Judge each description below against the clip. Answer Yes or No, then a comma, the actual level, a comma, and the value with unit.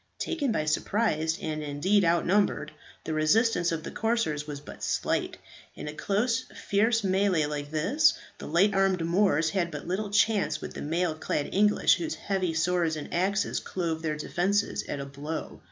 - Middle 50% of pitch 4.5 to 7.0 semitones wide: Yes, average, 4.8 semitones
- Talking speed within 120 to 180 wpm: Yes, average, 170 wpm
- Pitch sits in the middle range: Yes, medium, 175 Hz